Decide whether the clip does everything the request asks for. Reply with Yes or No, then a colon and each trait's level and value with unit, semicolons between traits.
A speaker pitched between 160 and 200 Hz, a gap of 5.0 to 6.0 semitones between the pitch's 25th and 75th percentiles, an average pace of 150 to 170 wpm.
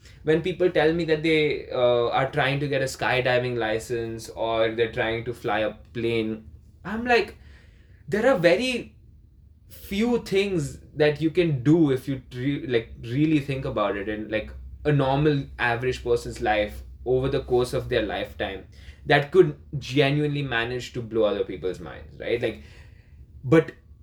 No: low, 125 Hz; wide, 5.6 semitones; average, 160 wpm